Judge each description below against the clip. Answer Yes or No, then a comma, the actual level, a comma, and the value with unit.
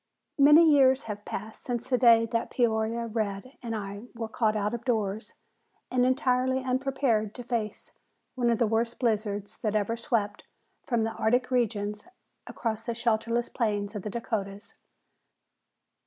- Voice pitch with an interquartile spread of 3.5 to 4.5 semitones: No, narrow, 2.6 semitones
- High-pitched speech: Yes, high, 230 Hz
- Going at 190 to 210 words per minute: No, average, 155 wpm